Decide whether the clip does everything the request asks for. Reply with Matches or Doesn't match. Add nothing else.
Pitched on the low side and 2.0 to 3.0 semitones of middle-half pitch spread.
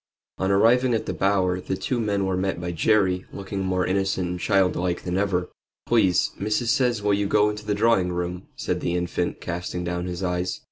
Matches